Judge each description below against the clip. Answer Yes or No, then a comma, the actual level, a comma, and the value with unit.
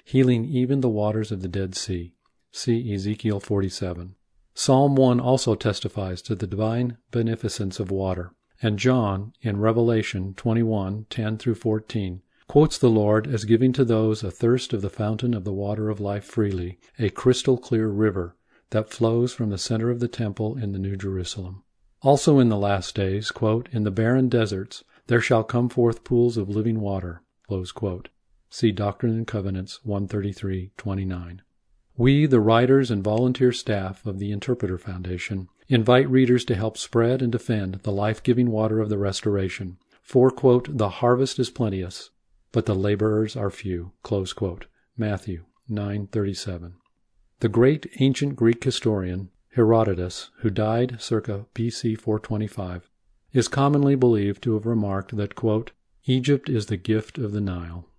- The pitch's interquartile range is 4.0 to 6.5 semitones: No, average, 3.4 semitones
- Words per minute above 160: No, average, 155 wpm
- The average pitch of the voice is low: Yes, low, 110 Hz